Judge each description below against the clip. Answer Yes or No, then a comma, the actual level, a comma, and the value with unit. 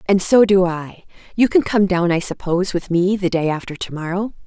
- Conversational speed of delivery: No, fast, 230 wpm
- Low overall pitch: No, medium, 185 Hz